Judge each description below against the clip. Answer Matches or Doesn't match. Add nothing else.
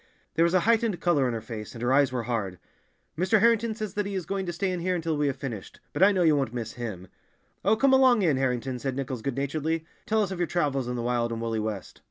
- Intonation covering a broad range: Matches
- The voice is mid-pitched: Matches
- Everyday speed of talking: Doesn't match